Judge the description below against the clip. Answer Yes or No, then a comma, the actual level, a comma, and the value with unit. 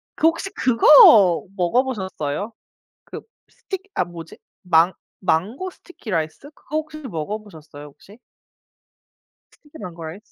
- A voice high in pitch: Yes, high, 200 Hz